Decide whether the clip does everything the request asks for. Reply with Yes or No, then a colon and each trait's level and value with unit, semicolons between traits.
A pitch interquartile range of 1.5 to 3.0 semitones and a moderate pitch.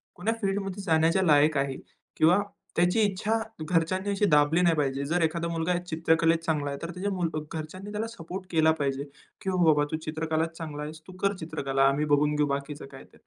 No: average, 3.4 semitones; medium, 160 Hz